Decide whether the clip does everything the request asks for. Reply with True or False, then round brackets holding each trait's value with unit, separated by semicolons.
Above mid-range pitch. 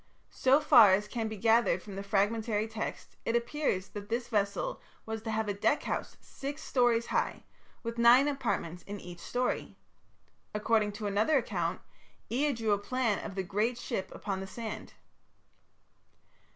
True (220 Hz)